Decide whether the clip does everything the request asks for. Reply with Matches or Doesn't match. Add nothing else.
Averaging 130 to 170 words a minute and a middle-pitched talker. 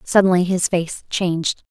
Matches